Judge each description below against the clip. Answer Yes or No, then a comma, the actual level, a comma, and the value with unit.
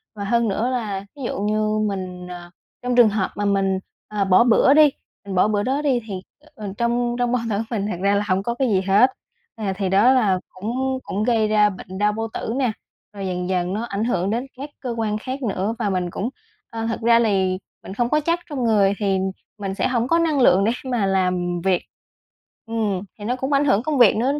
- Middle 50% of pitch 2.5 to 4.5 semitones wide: Yes, average, 3.9 semitones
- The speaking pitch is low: No, high, 215 Hz